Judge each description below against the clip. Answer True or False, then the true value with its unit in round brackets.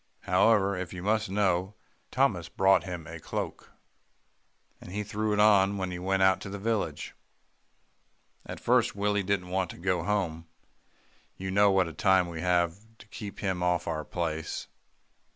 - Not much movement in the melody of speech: True (2.3 semitones)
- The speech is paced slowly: False (165 wpm)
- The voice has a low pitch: True (95 Hz)